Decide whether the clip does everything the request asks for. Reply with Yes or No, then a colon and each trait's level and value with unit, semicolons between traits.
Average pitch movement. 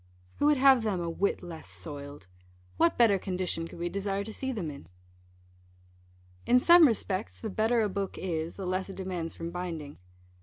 Yes: average, 4.6 semitones